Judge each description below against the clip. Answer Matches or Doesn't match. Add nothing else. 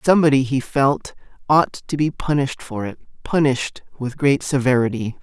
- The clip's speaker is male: Matches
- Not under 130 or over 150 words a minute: Matches